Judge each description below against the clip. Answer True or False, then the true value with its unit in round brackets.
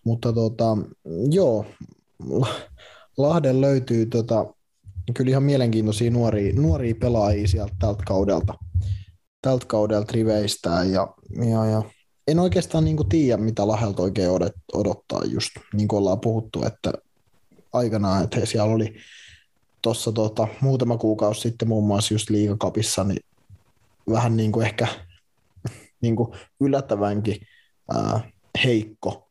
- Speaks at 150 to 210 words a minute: False (115 wpm)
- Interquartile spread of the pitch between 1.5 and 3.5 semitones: True (2.6 semitones)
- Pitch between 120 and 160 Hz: False (110 Hz)